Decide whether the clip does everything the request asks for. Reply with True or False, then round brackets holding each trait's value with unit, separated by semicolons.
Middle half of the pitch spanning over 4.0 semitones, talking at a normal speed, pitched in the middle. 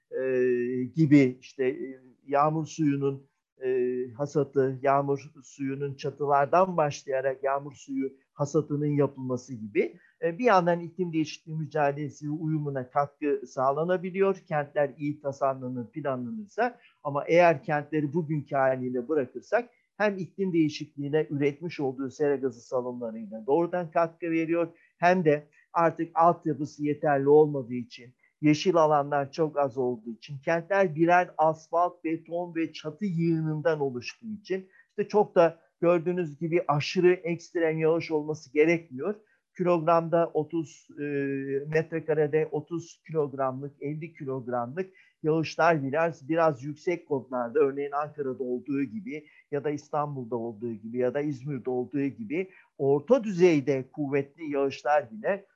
False (3.4 semitones; 120 wpm; 150 Hz)